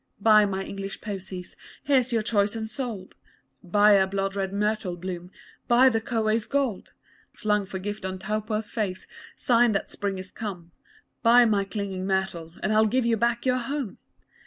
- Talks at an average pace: Yes, average, 165 wpm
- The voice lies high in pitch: Yes, high, 210 Hz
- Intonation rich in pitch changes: No, average, 3.0 semitones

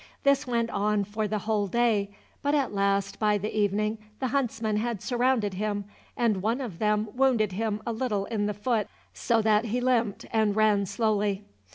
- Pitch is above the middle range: Yes, high, 215 Hz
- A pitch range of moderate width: No, narrow, 2.3 semitones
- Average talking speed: Yes, average, 185 wpm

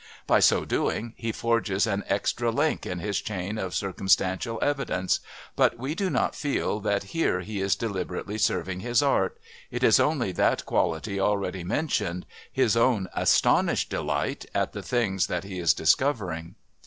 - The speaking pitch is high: No, low, 105 Hz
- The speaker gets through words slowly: No, average, 160 wpm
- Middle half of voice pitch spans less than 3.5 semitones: No, average, 4.1 semitones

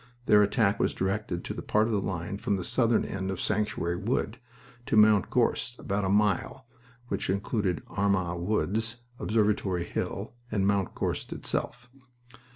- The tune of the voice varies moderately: No, narrow, 2.2 semitones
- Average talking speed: Yes, average, 160 wpm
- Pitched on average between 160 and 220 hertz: No, low, 100 Hz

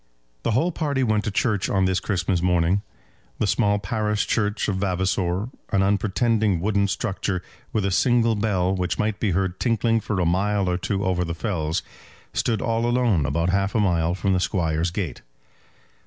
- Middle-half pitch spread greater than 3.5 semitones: No, average, 3.2 semitones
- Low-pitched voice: Yes, low, 100 Hz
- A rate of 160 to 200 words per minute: Yes, average, 180 wpm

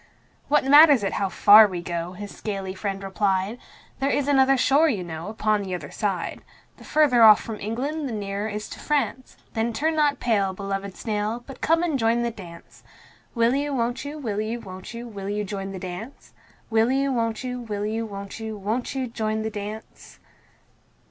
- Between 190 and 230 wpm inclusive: Yes, average, 195 wpm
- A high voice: Yes, high, 220 Hz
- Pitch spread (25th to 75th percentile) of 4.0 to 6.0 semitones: Yes, average, 4.3 semitones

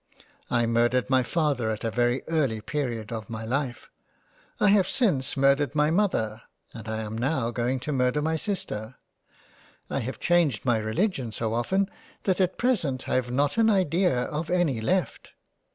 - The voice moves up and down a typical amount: No, wide, 6.0 semitones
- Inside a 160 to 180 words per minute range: Yes, average, 170 wpm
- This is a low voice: Yes, low, 130 Hz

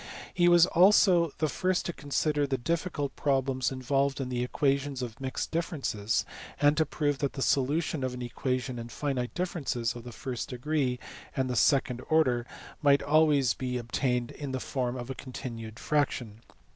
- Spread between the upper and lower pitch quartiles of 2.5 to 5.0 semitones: Yes, average, 3.2 semitones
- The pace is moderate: Yes, average, 170 wpm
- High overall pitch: No, low, 135 Hz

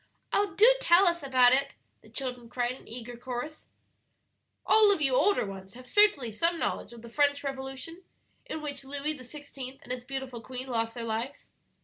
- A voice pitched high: Yes, very high, 265 Hz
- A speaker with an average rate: Yes, average, 180 wpm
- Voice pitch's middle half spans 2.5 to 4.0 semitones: Yes, average, 3.5 semitones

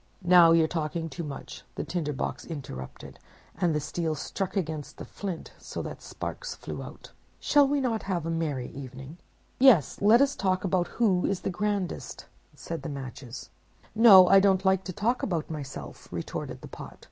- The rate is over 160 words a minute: Yes, average, 180 wpm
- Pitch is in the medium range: Yes, medium, 175 Hz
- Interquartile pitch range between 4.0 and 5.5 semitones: Yes, average, 4.5 semitones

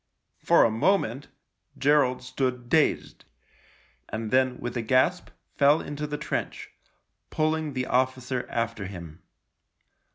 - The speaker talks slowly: Yes, slow, 120 wpm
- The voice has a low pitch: Yes, low, 130 Hz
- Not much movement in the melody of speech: No, average, 3.6 semitones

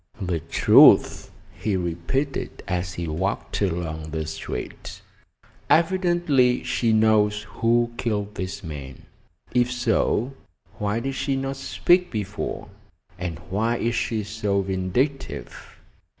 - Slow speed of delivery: Yes, slow, 115 wpm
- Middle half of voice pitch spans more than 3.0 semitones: Yes, average, 5.2 semitones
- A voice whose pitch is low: Yes, low, 105 Hz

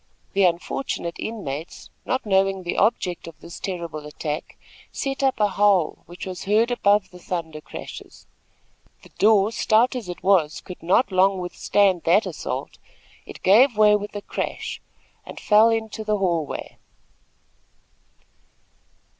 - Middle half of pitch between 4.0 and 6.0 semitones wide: No, average, 3.6 semitones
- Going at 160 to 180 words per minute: No, average, 145 wpm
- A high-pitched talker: Yes, high, 195 Hz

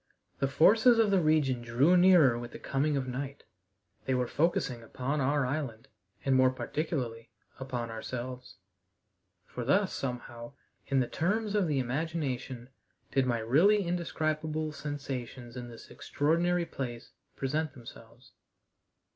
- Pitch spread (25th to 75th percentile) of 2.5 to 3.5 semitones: No, average, 4.2 semitones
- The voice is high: No, low, 135 Hz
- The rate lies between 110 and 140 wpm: Yes, slow, 135 wpm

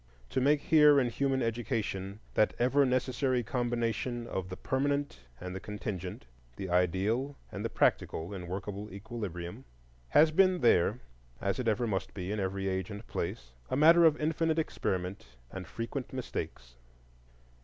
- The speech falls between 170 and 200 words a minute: No, average, 150 wpm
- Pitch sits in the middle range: No, low, 110 Hz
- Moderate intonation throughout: No, wide, 5.9 semitones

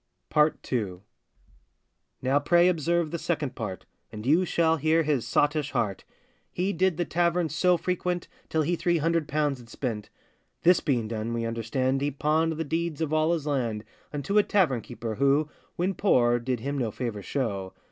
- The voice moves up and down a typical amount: No, wide, 5.7 semitones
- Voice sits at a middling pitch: Yes, medium, 145 Hz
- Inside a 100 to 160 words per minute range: No, average, 180 wpm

